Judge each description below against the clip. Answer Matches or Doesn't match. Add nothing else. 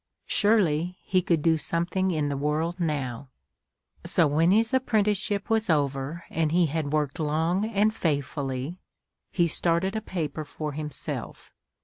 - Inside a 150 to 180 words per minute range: Doesn't match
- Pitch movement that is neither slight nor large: Matches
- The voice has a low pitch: Doesn't match